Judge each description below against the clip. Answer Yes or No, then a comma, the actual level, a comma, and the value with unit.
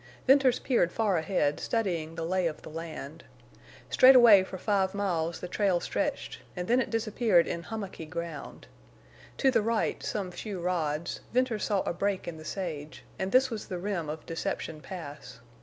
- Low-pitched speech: No, medium, 185 Hz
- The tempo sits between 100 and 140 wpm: No, average, 175 wpm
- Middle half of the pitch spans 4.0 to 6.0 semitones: Yes, average, 4.6 semitones